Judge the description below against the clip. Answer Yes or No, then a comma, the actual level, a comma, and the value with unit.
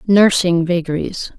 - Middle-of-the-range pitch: Yes, medium, 175 Hz